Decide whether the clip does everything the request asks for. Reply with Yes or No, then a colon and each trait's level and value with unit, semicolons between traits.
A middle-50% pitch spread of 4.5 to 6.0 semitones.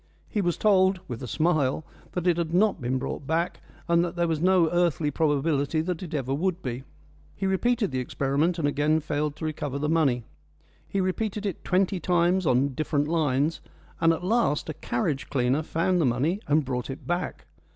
No: average, 4.1 semitones